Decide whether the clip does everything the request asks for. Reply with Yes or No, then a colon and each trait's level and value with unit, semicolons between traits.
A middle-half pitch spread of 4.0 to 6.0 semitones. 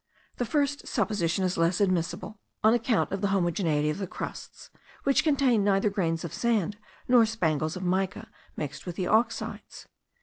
Yes: average, 4.4 semitones